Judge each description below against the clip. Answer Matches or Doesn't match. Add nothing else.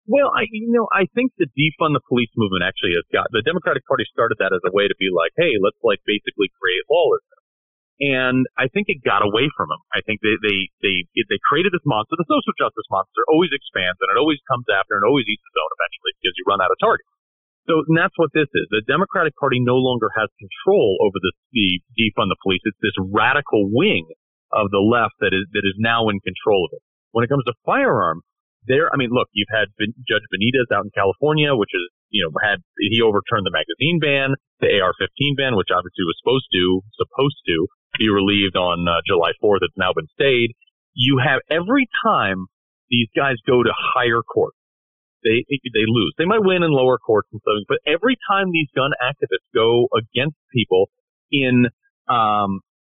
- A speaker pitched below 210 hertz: Matches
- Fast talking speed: Matches